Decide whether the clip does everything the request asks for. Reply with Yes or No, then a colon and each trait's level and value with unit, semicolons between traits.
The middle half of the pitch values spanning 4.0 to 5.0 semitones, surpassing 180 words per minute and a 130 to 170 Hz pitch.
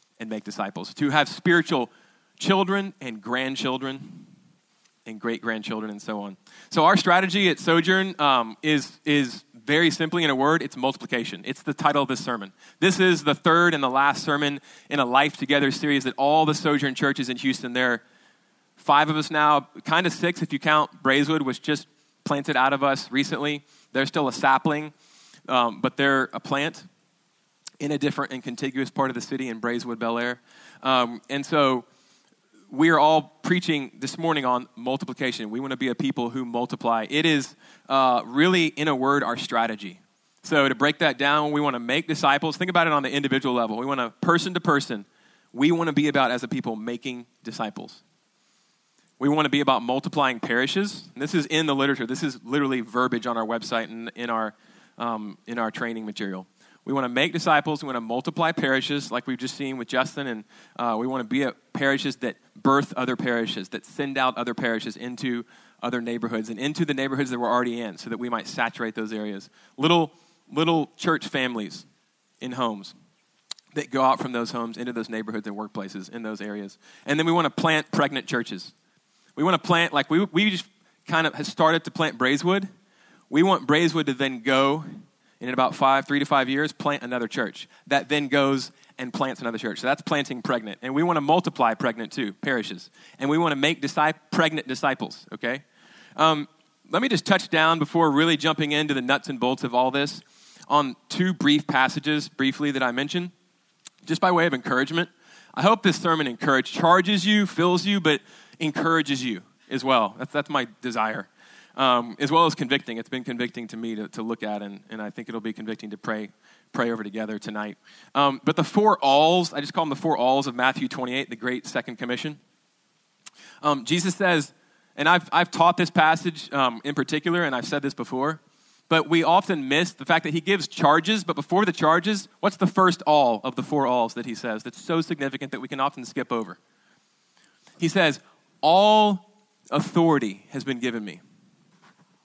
Yes: average, 4.6 semitones; average, 200 wpm; medium, 140 Hz